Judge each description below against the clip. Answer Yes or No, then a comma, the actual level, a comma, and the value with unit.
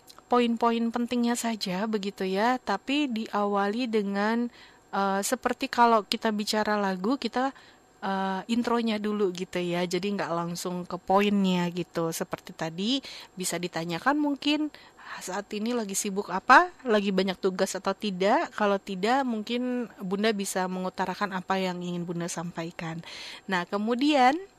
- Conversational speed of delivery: Yes, average, 130 wpm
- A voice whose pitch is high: Yes, high, 205 Hz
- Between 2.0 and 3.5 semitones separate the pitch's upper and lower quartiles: No, average, 4.1 semitones